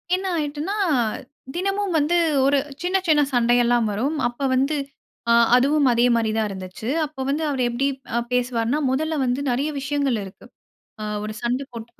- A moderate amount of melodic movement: Yes, average, 3.9 semitones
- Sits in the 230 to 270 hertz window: Yes, very high, 265 Hz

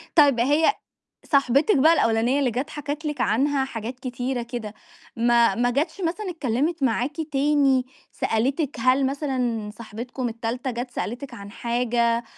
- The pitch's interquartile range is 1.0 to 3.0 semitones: No, average, 3.4 semitones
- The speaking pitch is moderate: No, very high, 255 Hz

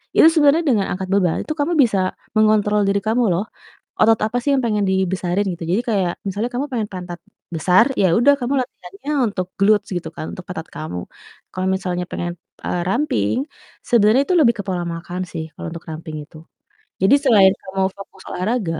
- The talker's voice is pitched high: Yes, high, 195 Hz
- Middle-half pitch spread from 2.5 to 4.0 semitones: No, average, 4.5 semitones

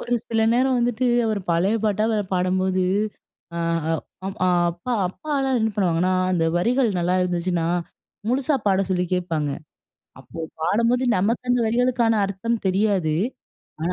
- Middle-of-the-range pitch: No, high, 200 Hz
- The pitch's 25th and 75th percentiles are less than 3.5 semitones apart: No, average, 4.8 semitones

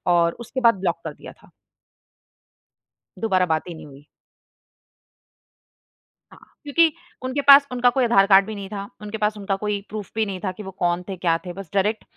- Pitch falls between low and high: No, high, 200 Hz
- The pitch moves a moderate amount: Yes, average, 3.7 semitones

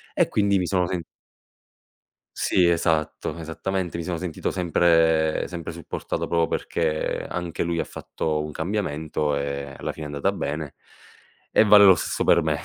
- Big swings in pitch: No, narrow, 2.5 semitones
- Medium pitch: No, very low, 85 Hz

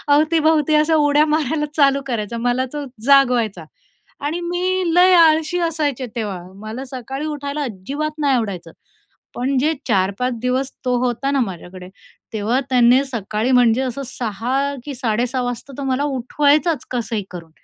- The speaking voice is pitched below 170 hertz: No, very high, 260 Hz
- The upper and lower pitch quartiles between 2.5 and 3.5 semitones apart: No, average, 4.3 semitones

